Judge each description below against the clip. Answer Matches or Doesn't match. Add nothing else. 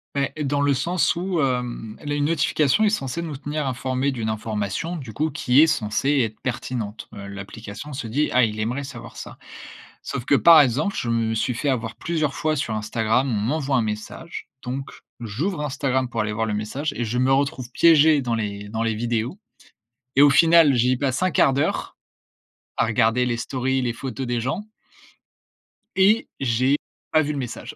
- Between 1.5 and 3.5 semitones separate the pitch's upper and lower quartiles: Doesn't match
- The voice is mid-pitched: Doesn't match